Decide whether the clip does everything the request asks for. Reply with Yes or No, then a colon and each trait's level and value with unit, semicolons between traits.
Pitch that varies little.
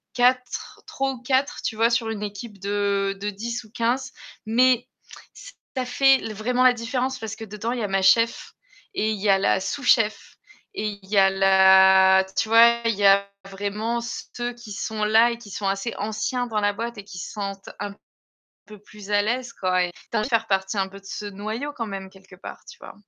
No: average, 3.2 semitones